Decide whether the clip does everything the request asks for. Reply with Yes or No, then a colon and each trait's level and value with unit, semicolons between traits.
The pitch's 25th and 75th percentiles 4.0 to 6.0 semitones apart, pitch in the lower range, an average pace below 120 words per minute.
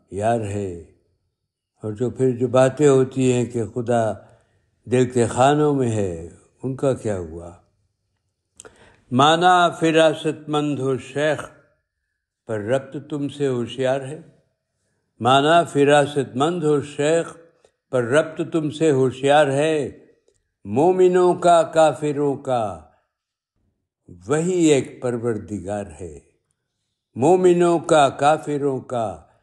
Yes: wide, 5.5 semitones; low, 130 Hz; slow, 110 wpm